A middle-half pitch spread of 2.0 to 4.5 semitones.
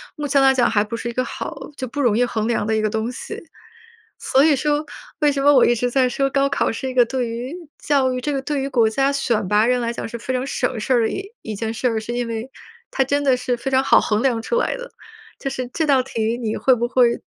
Yes: average, 2.9 semitones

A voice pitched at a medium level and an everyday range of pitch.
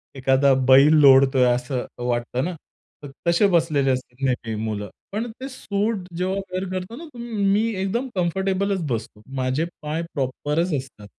No: medium, 150 Hz; wide, 6.8 semitones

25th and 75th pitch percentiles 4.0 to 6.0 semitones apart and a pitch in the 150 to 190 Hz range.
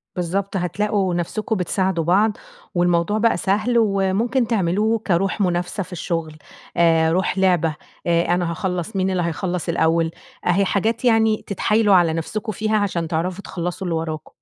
No: average, 3.6 semitones; medium, 185 Hz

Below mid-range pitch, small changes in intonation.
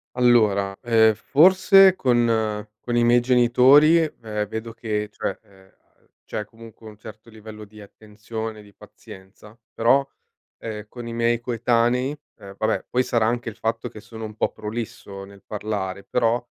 Yes: low, 115 Hz; narrow, 2.2 semitones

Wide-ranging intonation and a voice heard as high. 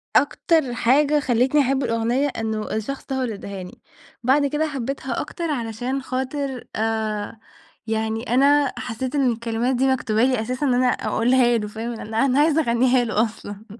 No: average, 3.4 semitones; very high, 250 Hz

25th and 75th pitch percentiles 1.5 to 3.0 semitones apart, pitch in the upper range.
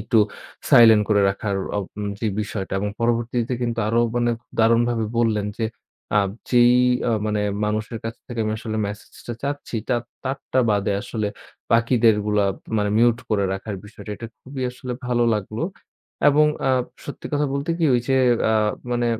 No: narrow, 2.4 semitones; low, 115 Hz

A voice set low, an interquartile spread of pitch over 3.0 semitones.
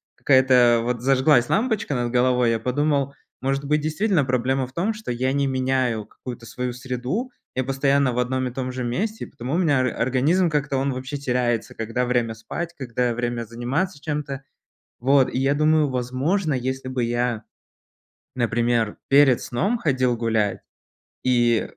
No: low, 130 Hz; average, 2.7 semitones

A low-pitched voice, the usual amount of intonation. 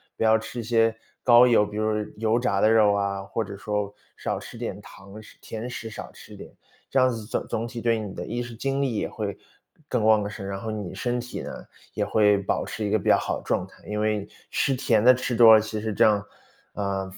No: low, 110 Hz; narrow, 2.2 semitones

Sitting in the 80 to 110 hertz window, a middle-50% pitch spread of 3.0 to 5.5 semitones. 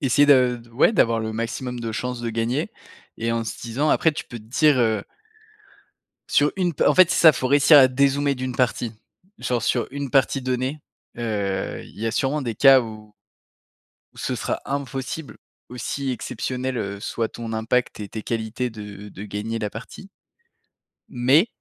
No: low, 125 Hz; average, 3.3 semitones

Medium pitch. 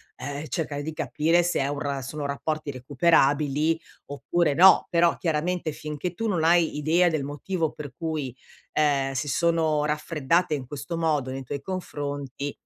Yes: medium, 150 Hz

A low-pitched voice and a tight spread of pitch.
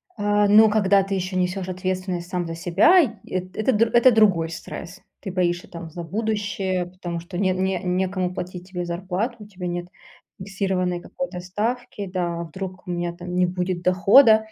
No: medium, 185 Hz; narrow, 2.3 semitones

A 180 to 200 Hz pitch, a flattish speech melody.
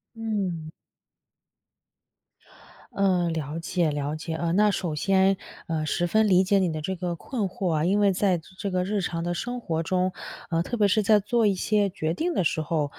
No: medium, 185 Hz; average, 3.6 semitones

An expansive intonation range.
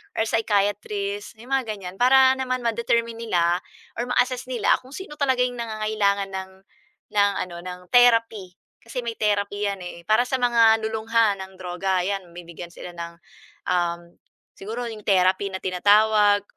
No: average, 3.7 semitones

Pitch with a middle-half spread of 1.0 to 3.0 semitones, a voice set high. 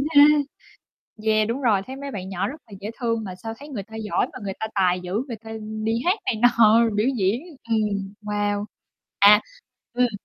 Yes: average, 2.7 semitones; high, 215 Hz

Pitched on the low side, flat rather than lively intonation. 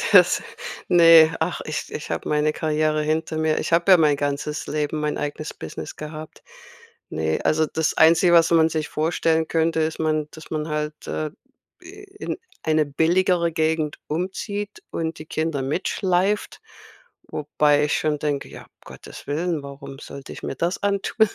No: medium, 155 Hz; narrow, 1.7 semitones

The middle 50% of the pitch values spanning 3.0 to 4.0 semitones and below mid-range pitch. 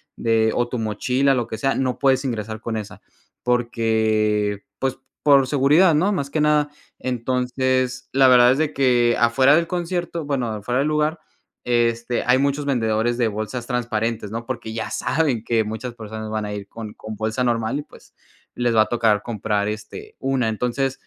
Yes: average, 3.4 semitones; low, 120 Hz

